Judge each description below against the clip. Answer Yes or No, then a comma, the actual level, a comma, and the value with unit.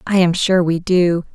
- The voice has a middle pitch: Yes, medium, 175 Hz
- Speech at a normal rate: No, fast, 225 wpm